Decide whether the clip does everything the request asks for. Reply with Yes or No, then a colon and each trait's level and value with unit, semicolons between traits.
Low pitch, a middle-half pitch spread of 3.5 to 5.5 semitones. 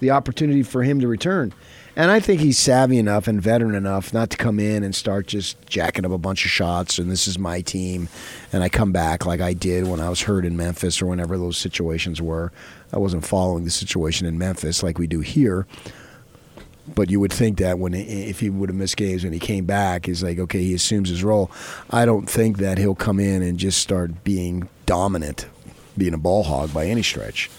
No: very low, 95 Hz; average, 2.8 semitones